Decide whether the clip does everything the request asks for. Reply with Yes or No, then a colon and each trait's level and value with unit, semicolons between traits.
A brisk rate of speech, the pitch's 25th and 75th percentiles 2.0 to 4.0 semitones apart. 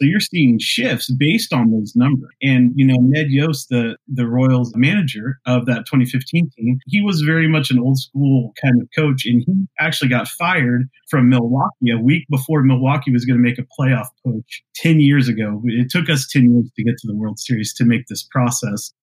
Yes: fast, 210 wpm; average, 2.8 semitones